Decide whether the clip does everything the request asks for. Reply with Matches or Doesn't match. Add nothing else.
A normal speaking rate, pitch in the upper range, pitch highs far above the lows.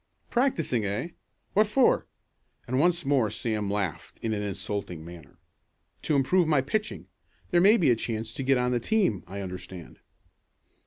Doesn't match